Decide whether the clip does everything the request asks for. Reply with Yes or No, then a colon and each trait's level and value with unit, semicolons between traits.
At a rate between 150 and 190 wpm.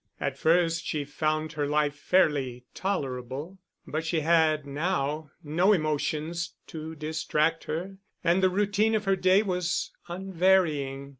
No: slow, 135 wpm